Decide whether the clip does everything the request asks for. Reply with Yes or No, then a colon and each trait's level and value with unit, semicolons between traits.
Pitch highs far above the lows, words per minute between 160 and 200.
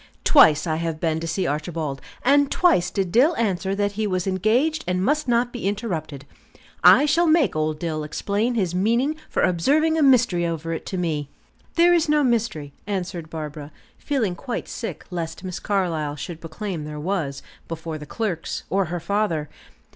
Yes: wide, 6.7 semitones; average, 175 wpm